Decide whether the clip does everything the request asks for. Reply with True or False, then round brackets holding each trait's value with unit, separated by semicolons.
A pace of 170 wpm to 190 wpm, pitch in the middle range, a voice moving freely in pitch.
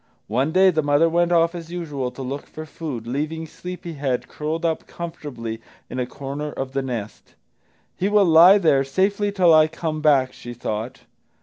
False (185 wpm; 155 Hz; 4.2 semitones)